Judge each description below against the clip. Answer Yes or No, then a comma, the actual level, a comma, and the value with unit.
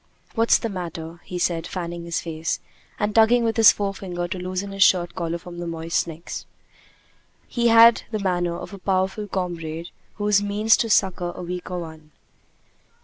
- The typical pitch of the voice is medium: Yes, medium, 180 Hz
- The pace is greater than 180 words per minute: No, average, 170 wpm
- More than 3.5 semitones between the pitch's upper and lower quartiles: No, average, 3.1 semitones